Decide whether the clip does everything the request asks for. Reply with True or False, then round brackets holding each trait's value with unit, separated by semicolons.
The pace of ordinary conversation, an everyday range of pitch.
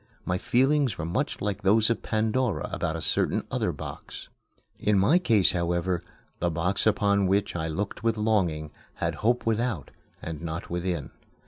True (160 wpm; 4.5 semitones)